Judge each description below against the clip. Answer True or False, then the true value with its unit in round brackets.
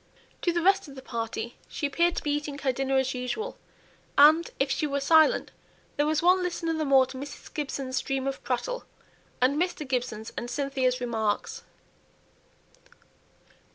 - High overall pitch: True (275 Hz)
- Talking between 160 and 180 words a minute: True (165 wpm)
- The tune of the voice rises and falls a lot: False (3.6 semitones)